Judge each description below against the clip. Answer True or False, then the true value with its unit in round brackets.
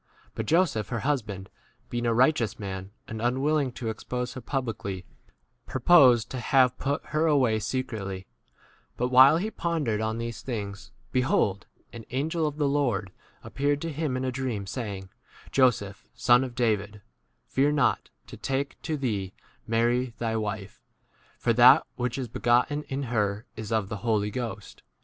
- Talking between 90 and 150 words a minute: False (175 wpm)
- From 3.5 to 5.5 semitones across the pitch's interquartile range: True (3.9 semitones)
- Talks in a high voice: False (120 Hz)